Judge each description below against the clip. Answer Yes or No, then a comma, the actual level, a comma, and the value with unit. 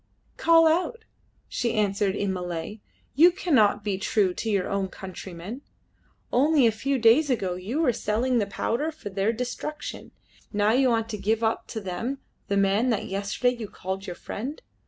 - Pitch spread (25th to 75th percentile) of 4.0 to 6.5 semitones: Yes, average, 4.5 semitones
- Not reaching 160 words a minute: No, average, 180 wpm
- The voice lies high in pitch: Yes, high, 220 Hz